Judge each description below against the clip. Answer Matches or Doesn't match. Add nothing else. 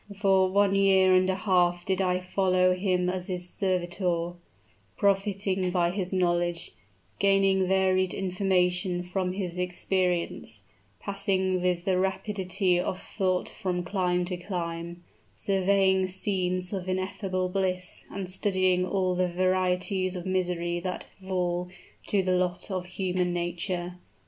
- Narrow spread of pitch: Matches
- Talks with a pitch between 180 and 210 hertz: Matches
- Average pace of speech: Doesn't match